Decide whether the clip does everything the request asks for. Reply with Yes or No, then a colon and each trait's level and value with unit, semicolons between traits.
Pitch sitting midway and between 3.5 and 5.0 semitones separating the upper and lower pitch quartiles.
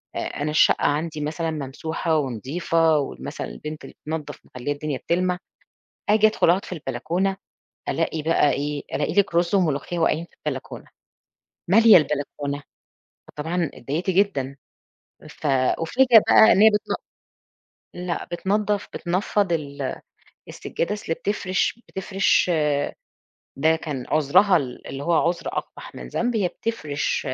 Yes: medium, 165 Hz; average, 4.4 semitones